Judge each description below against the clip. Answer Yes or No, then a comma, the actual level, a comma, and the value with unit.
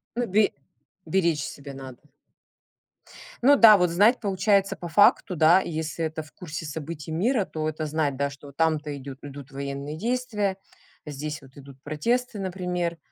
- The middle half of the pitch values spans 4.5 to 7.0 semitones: Yes, average, 4.9 semitones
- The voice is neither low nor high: Yes, medium, 160 Hz